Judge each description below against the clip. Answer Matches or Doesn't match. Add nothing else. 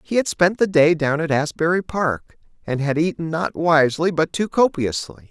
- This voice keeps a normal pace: Matches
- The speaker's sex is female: Doesn't match